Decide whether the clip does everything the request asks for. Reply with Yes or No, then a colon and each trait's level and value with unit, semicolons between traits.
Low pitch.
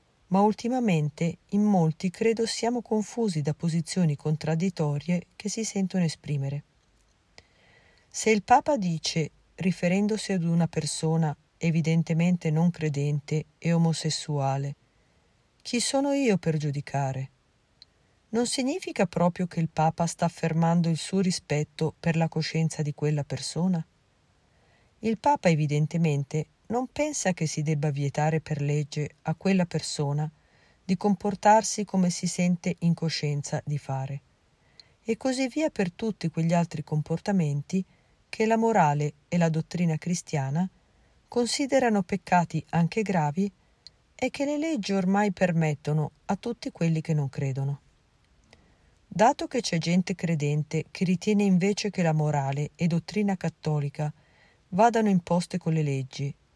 No: medium, 170 Hz